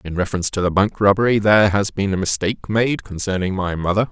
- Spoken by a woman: No, male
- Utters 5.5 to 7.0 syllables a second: Yes, 6.4 syllables/s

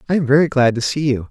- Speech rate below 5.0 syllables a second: No, 7.1 syllables/s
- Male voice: Yes, male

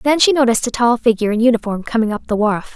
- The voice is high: Yes, high, 230 Hz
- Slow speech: No, fast, 260 wpm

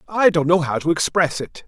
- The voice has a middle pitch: Yes, medium, 165 Hz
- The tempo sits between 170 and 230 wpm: No, fast, 250 wpm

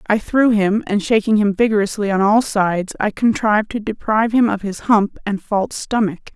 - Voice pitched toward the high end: Yes, high, 210 Hz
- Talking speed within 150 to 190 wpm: No, average, 200 wpm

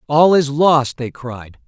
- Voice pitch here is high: No, medium, 140 Hz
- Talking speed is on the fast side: No, average, 180 wpm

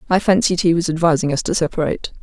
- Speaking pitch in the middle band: Yes, medium, 170 Hz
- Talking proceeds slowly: No, fast, 215 wpm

